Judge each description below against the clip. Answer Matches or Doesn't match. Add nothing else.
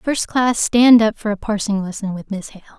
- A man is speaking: Doesn't match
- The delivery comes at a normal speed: Doesn't match